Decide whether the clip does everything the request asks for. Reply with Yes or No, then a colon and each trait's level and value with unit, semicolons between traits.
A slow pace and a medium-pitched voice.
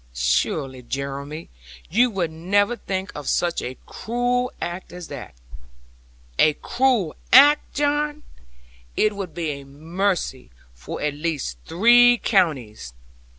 Yes: slow, 120 wpm; medium, 175 Hz